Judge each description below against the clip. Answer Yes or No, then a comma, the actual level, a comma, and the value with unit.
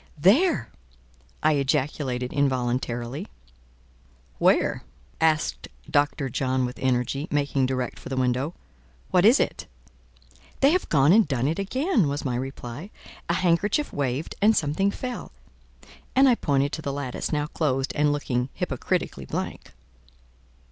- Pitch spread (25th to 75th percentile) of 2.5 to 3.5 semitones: No, average, 5.1 semitones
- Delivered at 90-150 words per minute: Yes, slow, 135 wpm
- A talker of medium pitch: Yes, medium, 145 Hz